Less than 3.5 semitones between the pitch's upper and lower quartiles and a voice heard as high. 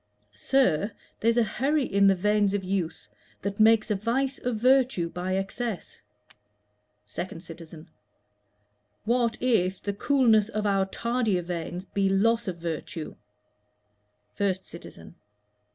No: average, 4.1 semitones; high, 200 Hz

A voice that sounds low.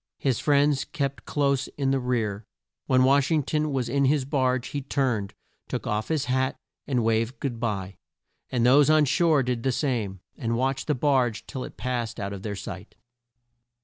Yes: low, 130 Hz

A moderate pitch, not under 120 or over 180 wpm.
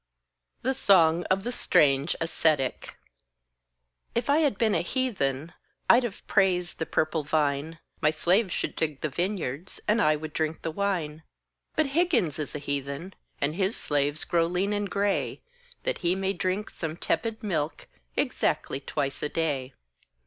Yes: medium, 170 Hz; average, 155 wpm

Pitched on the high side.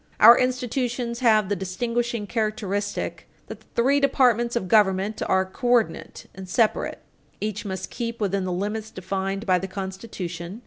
Yes: high, 210 Hz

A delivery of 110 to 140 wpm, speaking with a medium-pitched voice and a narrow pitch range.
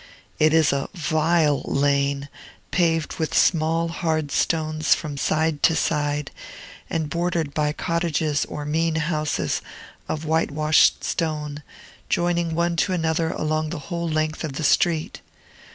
Yes: slow, 135 wpm; medium, 155 Hz; narrow, 1.7 semitones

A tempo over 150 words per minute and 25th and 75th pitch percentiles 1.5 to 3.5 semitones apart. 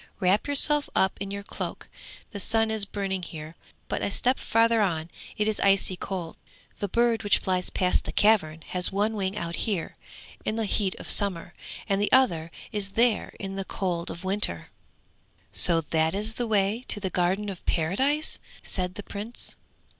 Yes: average, 180 wpm; average, 3.2 semitones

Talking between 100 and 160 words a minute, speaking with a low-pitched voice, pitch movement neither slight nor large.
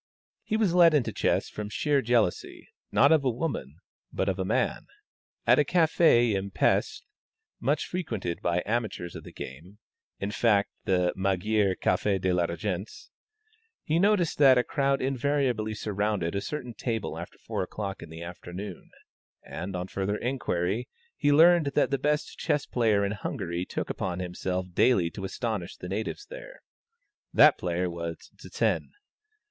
No: average, 155 wpm; low, 105 Hz; wide, 6.9 semitones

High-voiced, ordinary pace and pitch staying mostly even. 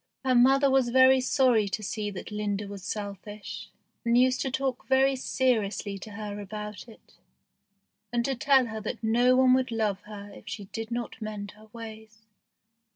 No: high, 225 Hz; average, 175 wpm; average, 3.4 semitones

